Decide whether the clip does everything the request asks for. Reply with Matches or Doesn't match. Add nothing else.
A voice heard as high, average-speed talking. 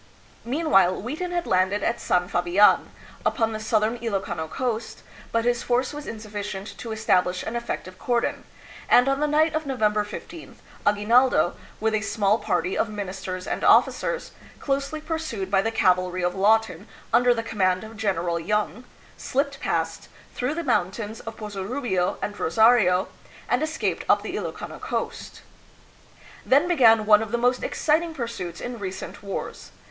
Matches